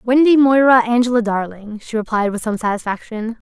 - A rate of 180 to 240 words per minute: No, average, 155 wpm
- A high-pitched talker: Yes, high, 230 Hz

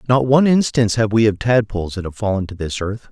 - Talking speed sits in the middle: No, fast, 250 wpm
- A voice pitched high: No, low, 110 Hz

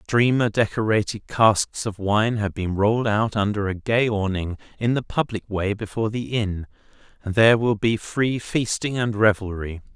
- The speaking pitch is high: No, low, 105 Hz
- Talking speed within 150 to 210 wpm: Yes, average, 170 wpm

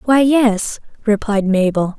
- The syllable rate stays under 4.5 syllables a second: Yes, 3.8 syllables/s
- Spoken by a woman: Yes, female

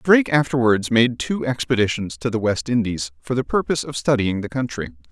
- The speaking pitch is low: Yes, low, 115 Hz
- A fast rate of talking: No, average, 190 wpm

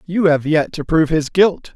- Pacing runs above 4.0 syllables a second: Yes, 4.9 syllables/s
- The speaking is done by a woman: No, male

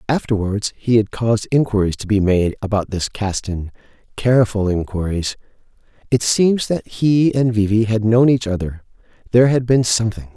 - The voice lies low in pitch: Yes, low, 110 Hz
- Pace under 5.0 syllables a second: No, 5.1 syllables/s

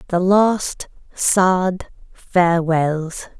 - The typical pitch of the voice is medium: Yes, medium, 180 Hz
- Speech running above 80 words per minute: No, slow, 70 wpm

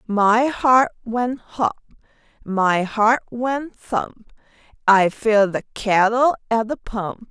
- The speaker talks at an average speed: No, slow, 125 wpm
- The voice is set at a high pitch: Yes, high, 225 Hz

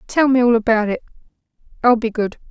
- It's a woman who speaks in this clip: Yes, female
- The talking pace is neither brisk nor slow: Yes, average, 190 wpm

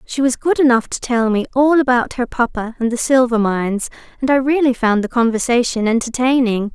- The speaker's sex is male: No, female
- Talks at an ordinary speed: Yes, average, 195 wpm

